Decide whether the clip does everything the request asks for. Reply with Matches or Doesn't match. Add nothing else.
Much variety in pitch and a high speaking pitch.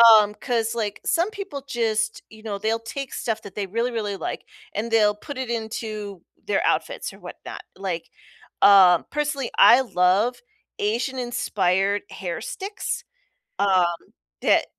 Doesn't match